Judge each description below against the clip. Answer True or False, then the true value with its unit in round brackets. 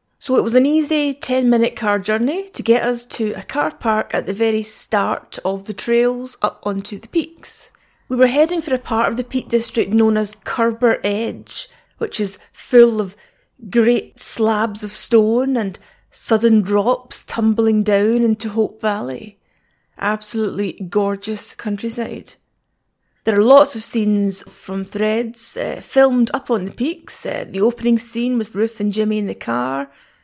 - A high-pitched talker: True (225 Hz)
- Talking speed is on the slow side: False (165 wpm)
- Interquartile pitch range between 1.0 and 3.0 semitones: True (2.5 semitones)